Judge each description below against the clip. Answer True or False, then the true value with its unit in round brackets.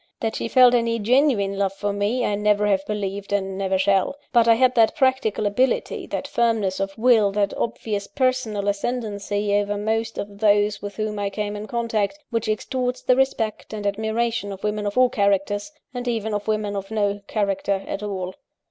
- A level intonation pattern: True (2.3 semitones)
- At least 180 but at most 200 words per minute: True (190 wpm)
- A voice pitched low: False (210 Hz)